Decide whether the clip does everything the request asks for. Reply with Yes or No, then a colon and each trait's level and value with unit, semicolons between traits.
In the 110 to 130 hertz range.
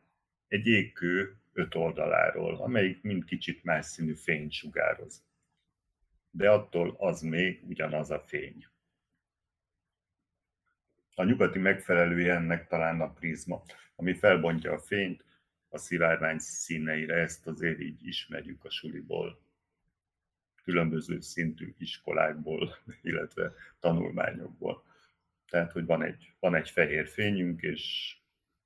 No: very low, 85 Hz